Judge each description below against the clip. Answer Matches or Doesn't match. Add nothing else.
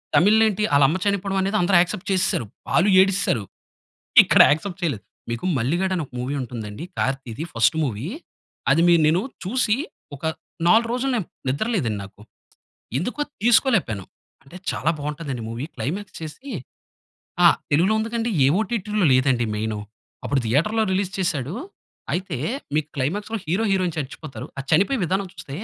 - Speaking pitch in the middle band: Matches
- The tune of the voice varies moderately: Doesn't match